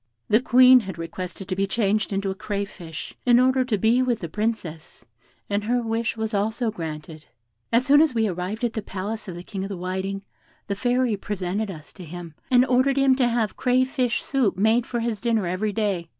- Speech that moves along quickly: Yes, fast, 210 wpm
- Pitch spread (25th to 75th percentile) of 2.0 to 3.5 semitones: No, average, 4.3 semitones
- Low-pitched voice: No, high, 215 Hz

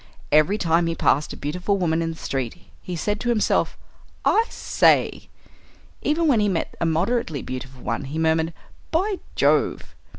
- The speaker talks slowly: No, average, 165 wpm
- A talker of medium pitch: Yes, medium, 165 Hz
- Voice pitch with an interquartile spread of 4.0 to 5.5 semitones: Yes, average, 5.0 semitones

